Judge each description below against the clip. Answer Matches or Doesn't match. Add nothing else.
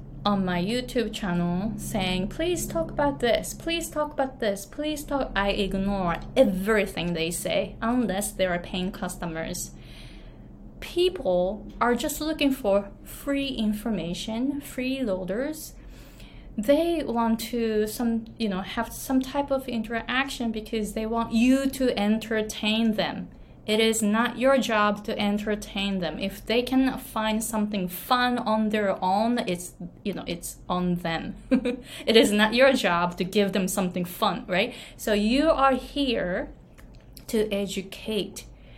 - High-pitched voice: Matches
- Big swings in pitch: Doesn't match